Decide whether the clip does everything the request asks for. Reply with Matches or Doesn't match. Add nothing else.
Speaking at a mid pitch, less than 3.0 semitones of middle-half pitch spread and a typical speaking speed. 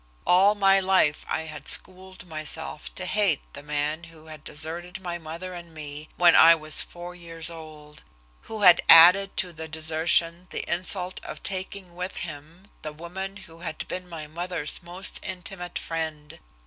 Matches